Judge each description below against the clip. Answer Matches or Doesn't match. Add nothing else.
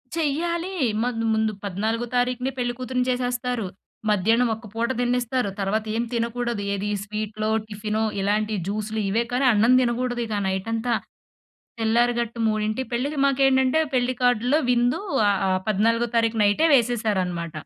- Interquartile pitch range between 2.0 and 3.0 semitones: Matches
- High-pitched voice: Matches